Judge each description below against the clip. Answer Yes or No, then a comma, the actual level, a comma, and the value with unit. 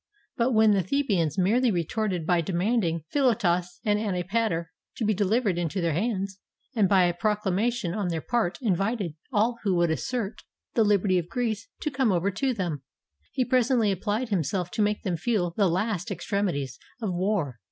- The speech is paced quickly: No, average, 185 wpm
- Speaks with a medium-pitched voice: No, high, 200 Hz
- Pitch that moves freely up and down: No, average, 4.2 semitones